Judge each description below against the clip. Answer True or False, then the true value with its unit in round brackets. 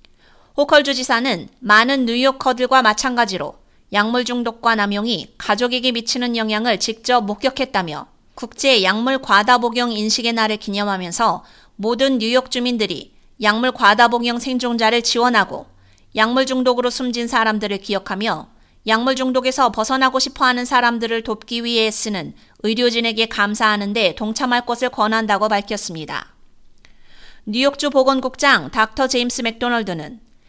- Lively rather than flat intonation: False (2.9 semitones)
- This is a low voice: False (235 Hz)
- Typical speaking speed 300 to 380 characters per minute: True (325 characters per minute)